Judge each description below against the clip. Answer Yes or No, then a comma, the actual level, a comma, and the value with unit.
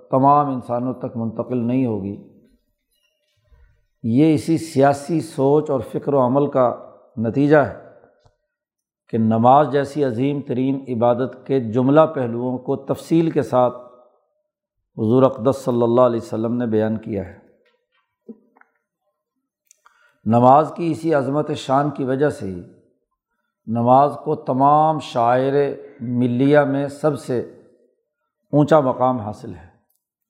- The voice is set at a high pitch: No, low, 135 Hz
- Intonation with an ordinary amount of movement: Yes, average, 3.5 semitones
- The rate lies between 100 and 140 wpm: Yes, average, 120 wpm